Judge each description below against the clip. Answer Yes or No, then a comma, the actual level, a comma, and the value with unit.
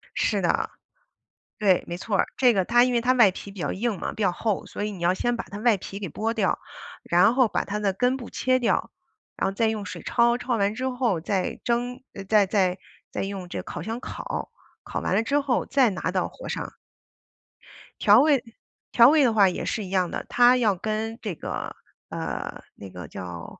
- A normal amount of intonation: Yes, average, 4.0 semitones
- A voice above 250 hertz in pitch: No, high, 215 Hz